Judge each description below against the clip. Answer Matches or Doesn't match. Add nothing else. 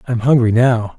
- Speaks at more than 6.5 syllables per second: Doesn't match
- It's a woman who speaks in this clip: Doesn't match